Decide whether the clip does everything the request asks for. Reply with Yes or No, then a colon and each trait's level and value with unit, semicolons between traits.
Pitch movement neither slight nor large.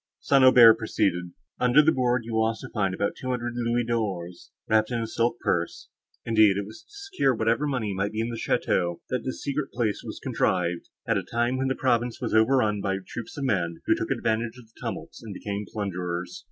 Yes: average, 3.6 semitones